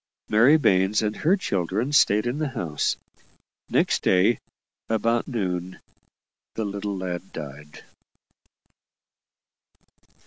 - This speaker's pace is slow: Yes, slow, 100 wpm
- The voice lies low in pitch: Yes, low, 100 Hz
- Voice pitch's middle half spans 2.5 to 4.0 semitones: No, average, 4.4 semitones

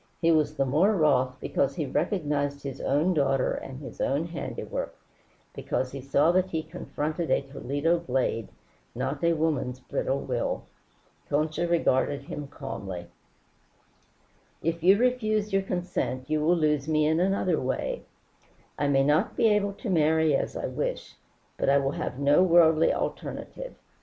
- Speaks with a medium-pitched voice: Yes, medium, 155 Hz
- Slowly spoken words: No, average, 155 wpm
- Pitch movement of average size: Yes, average, 3.8 semitones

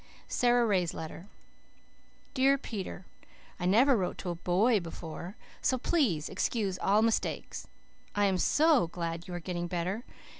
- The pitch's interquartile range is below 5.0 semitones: No, wide, 5.4 semitones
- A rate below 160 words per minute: Yes, average, 145 wpm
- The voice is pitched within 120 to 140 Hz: No, high, 190 Hz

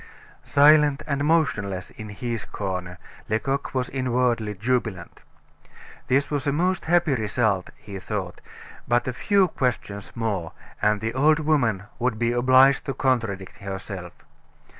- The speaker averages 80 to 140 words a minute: Yes, slow, 135 wpm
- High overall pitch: No, low, 120 Hz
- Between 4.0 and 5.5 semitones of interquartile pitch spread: Yes, average, 5.2 semitones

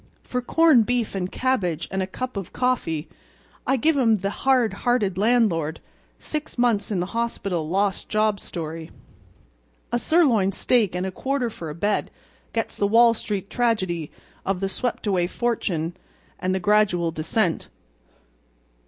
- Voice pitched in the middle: No, high, 205 Hz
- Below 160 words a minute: Yes, average, 150 wpm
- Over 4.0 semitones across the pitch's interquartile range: Yes, average, 5.0 semitones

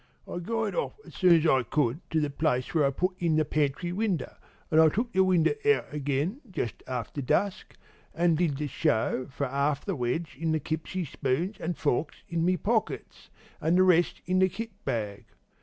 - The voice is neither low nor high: Yes, medium, 160 Hz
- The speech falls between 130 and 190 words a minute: No, average, 200 wpm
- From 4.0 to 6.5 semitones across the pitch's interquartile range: Yes, average, 4.6 semitones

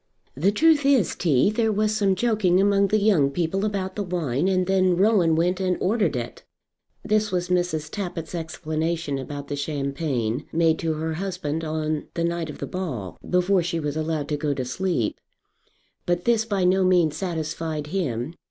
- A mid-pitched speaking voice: Yes, medium, 175 Hz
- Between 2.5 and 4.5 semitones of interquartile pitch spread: Yes, average, 3.9 semitones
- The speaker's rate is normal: Yes, average, 180 wpm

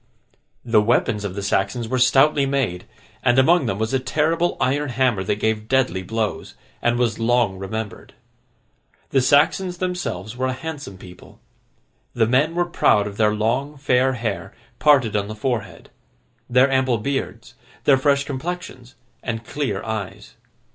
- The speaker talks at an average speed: Yes, average, 155 wpm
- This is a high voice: No, low, 125 Hz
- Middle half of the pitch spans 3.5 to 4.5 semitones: Yes, average, 4.2 semitones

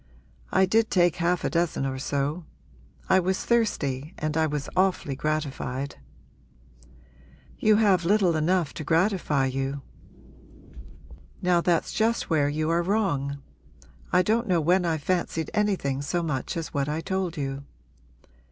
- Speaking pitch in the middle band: Yes, medium, 165 Hz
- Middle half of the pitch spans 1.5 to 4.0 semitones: No, average, 4.6 semitones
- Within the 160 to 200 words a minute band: No, average, 145 wpm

